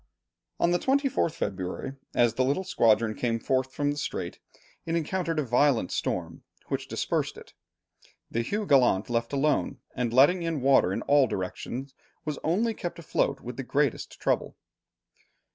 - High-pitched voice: No, low, 135 Hz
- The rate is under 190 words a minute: Yes, average, 160 wpm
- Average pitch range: No, wide, 5.7 semitones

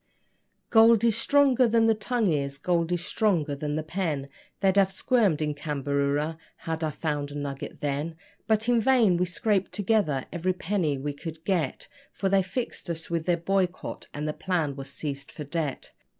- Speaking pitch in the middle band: Yes, medium, 170 Hz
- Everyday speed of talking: Yes, average, 180 wpm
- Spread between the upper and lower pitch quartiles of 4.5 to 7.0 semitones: Yes, wide, 5.4 semitones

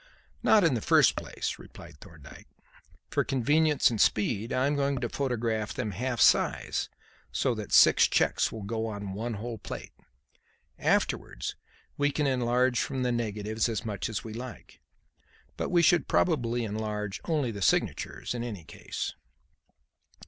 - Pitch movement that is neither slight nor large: Yes, average, 3.6 semitones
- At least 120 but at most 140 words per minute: No, average, 155 wpm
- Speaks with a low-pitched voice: Yes, low, 115 Hz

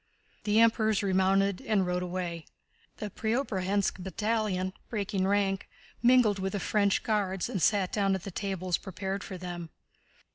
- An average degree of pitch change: No, narrow, 2.1 semitones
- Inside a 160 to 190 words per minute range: No, average, 145 wpm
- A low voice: No, high, 195 Hz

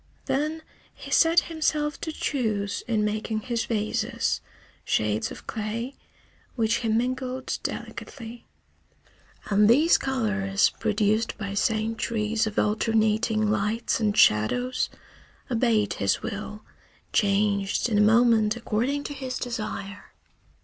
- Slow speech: Yes, slow, 115 wpm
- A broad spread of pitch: No, average, 2.8 semitones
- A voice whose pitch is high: Yes, high, 220 Hz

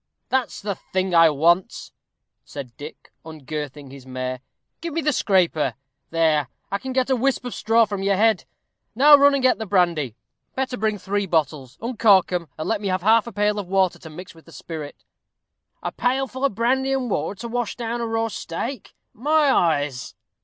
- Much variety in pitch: Yes, wide, 7.1 semitones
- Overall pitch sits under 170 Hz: No, high, 200 Hz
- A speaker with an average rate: Yes, average, 195 wpm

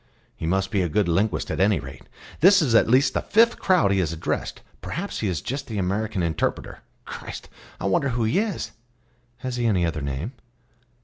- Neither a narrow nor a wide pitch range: No, wide, 6.7 semitones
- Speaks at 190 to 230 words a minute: Yes, average, 200 wpm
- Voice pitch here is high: No, low, 105 Hz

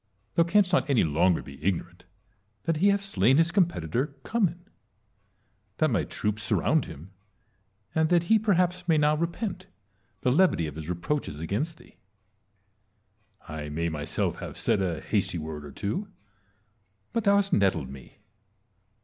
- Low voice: No, medium, 145 Hz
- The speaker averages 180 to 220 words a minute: No, average, 150 wpm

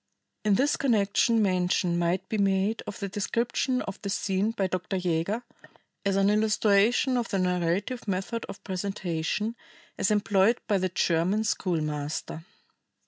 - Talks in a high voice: Yes, high, 195 Hz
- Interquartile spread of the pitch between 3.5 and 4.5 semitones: No, average, 3.0 semitones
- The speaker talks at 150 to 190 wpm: No, average, 140 wpm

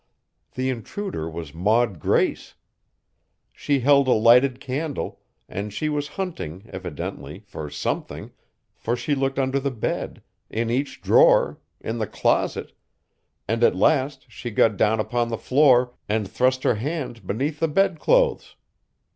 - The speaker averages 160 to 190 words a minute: No, average, 140 wpm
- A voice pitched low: Yes, low, 130 Hz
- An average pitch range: Yes, average, 5.0 semitones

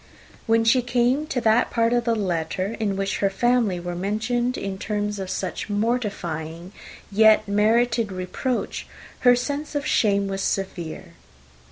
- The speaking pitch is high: Yes, high, 210 Hz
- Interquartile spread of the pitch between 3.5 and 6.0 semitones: Yes, average, 3.9 semitones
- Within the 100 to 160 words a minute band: Yes, average, 150 wpm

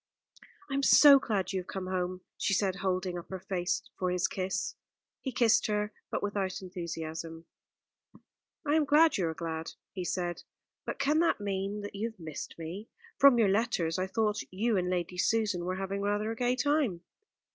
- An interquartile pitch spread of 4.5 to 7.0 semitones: No, average, 3.7 semitones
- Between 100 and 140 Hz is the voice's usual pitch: No, high, 195 Hz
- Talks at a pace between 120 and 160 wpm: No, average, 190 wpm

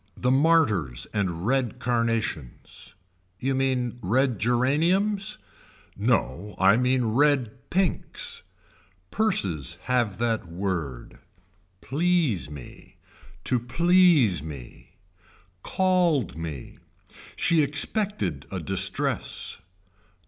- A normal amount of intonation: No, wide, 8.0 semitones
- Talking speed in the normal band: No, slow, 85 wpm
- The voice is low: Yes, low, 125 Hz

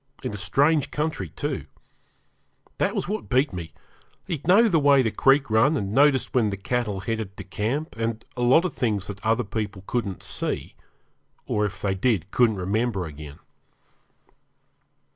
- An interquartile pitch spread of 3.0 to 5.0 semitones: No, wide, 5.6 semitones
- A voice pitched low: Yes, low, 115 Hz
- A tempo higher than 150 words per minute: Yes, average, 165 wpm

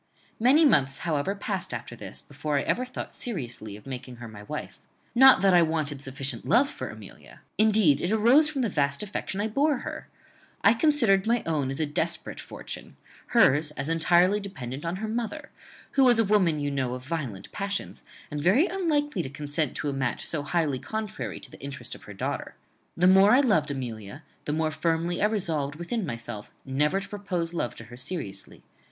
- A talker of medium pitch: Yes, medium, 165 Hz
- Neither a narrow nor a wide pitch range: No, wide, 7.4 semitones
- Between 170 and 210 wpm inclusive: Yes, average, 195 wpm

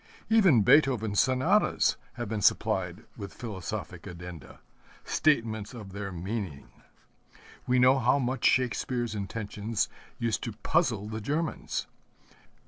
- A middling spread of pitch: Yes, average, 4.2 semitones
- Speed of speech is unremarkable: No, slow, 115 wpm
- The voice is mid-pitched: No, low, 115 Hz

